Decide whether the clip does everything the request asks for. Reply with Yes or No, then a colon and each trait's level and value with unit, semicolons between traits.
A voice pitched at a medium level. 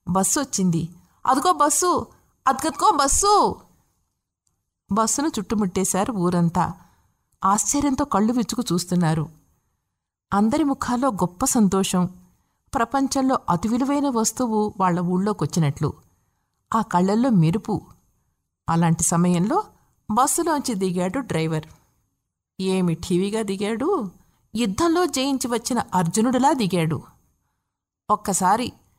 No: high, 210 Hz